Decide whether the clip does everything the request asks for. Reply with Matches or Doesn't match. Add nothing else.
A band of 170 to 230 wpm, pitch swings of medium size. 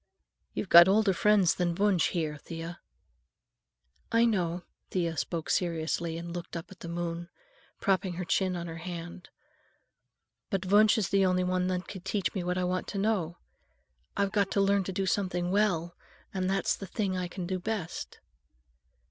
Doesn't match